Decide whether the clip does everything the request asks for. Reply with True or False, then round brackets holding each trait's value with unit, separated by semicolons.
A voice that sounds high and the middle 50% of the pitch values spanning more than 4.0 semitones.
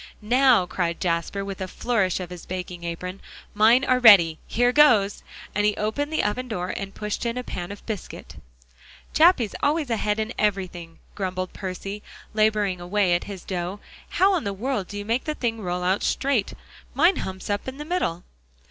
True (205 Hz; 4.8 semitones)